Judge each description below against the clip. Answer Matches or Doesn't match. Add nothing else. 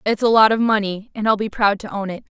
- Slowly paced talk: Doesn't match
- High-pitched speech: Matches